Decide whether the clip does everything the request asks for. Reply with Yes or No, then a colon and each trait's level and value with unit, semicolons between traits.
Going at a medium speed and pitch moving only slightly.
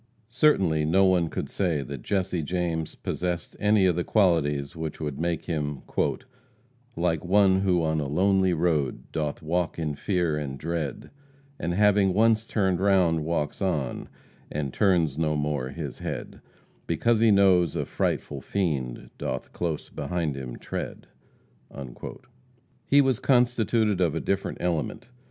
No: average, 145 wpm; average, 4.2 semitones